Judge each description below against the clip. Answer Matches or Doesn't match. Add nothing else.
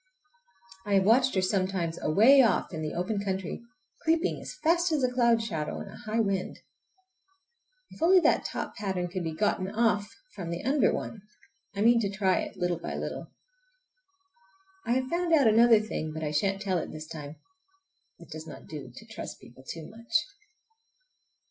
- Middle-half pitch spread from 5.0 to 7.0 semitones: Matches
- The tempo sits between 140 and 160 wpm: Doesn't match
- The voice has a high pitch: Matches